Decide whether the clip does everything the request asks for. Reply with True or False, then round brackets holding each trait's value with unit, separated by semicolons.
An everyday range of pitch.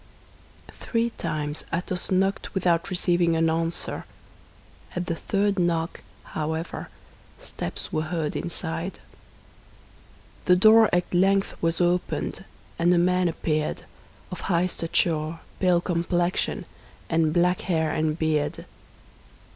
False (2.0 semitones)